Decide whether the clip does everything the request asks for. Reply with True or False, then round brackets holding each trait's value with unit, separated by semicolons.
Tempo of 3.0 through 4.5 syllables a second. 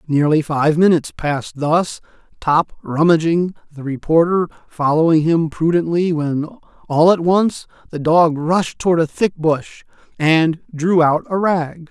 True (4.2 syllables/s)